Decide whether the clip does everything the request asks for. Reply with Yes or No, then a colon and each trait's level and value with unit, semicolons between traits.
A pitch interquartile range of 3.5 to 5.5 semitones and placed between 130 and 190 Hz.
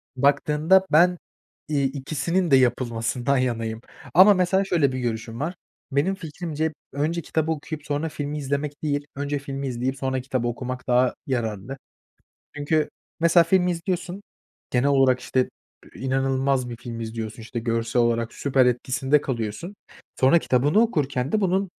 Yes: average, 4.2 semitones; medium, 140 Hz